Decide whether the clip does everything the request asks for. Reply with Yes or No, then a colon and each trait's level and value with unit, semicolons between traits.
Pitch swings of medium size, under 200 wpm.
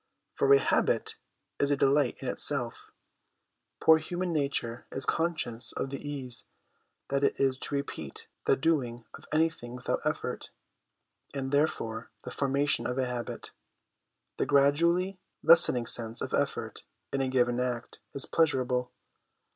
Yes: average, 3.6 semitones; average, 140 wpm